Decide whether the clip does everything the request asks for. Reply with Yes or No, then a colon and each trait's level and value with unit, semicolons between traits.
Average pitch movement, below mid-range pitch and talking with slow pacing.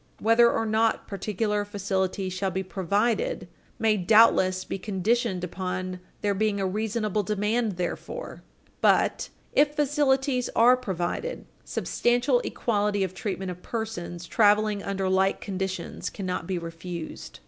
No: average, 3.4 semitones; high, 205 Hz; slow, 125 wpm